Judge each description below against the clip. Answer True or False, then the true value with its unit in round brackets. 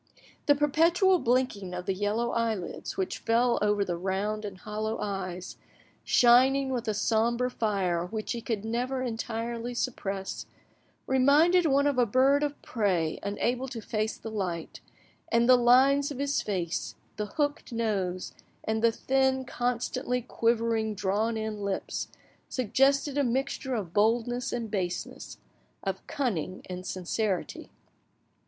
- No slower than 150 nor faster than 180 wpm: False (140 wpm)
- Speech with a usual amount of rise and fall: True (4.0 semitones)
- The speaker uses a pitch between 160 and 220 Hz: False (230 Hz)